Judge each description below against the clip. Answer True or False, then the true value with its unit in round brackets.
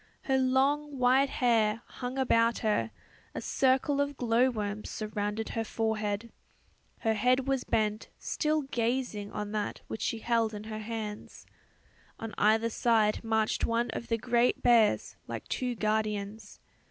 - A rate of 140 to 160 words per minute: True (145 wpm)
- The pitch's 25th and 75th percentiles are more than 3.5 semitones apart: False (2.8 semitones)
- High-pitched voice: True (230 Hz)